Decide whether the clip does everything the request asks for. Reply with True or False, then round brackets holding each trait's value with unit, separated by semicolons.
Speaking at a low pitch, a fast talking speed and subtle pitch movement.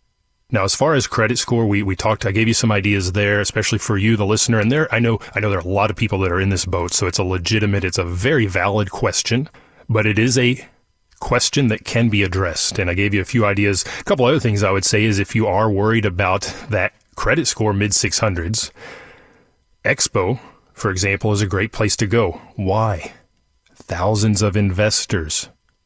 True (105 Hz; 215 wpm; 2.3 semitones)